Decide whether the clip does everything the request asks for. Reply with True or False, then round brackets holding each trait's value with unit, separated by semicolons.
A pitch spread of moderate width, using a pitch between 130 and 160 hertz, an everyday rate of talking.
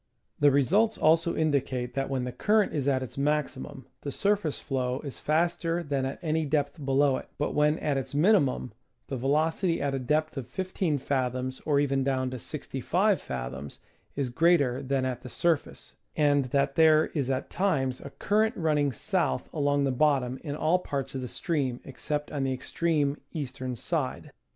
True (3.2 semitones; 140 Hz; 180 wpm)